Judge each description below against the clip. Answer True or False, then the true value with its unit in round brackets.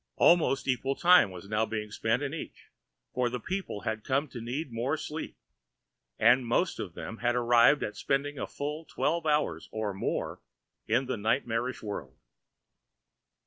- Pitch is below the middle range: True (125 Hz)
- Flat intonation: False (4.6 semitones)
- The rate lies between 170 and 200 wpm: False (155 wpm)